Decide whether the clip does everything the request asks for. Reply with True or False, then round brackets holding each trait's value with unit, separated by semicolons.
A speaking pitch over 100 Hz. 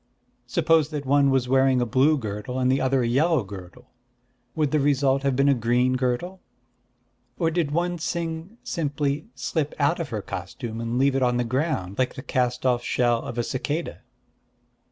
True (135 Hz)